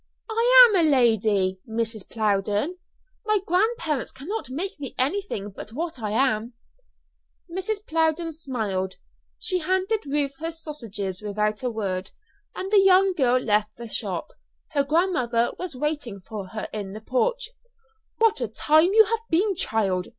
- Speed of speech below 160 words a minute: Yes, average, 150 wpm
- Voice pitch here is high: Yes, very high, 275 Hz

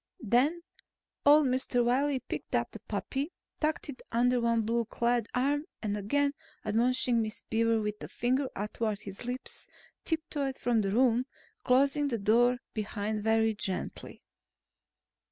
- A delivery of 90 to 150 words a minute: Yes, average, 140 wpm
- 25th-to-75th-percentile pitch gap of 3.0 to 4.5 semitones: Yes, average, 3.4 semitones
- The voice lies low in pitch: No, high, 240 Hz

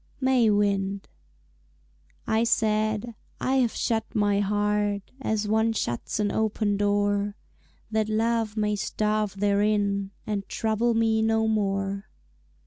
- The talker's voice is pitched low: No, high, 210 Hz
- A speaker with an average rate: No, slow, 120 wpm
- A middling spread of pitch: No, narrow, 1.4 semitones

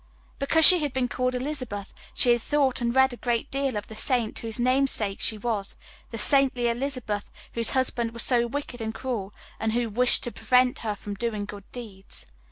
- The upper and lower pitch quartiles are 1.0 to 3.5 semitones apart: Yes, average, 2.9 semitones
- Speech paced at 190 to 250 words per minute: Yes, average, 195 wpm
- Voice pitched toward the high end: Yes, high, 240 Hz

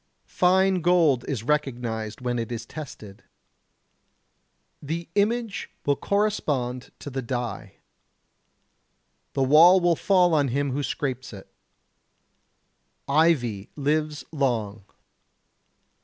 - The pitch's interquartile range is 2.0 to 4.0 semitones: No, wide, 5.6 semitones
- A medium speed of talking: No, slow, 100 wpm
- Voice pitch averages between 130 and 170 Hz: Yes, medium, 140 Hz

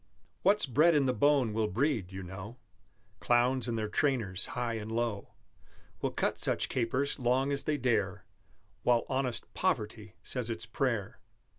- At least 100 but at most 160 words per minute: Yes, average, 155 wpm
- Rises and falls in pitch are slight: No, average, 3.8 semitones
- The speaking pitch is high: No, low, 120 Hz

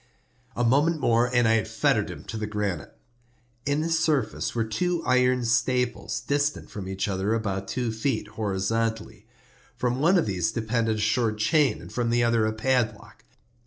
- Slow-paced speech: No, average, 170 wpm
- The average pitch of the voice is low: Yes, low, 115 Hz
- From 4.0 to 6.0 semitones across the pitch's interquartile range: No, average, 2.9 semitones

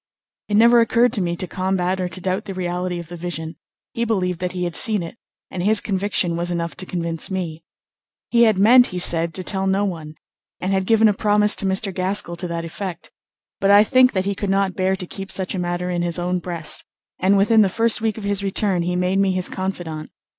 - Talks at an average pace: No, fast, 235 wpm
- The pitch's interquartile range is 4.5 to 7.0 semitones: No, narrow, 2.4 semitones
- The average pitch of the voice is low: No, medium, 185 Hz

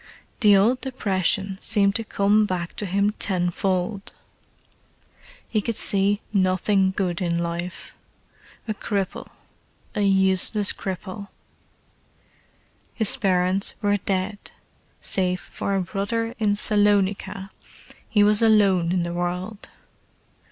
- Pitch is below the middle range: No, high, 195 Hz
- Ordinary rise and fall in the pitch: No, narrow, 2.0 semitones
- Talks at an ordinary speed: No, slow, 110 wpm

